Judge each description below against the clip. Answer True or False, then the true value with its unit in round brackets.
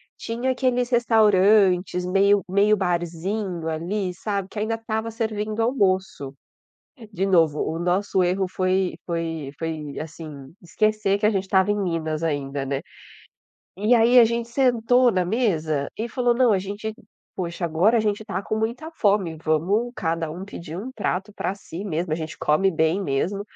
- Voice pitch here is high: True (195 Hz)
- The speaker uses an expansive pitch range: False (4.6 semitones)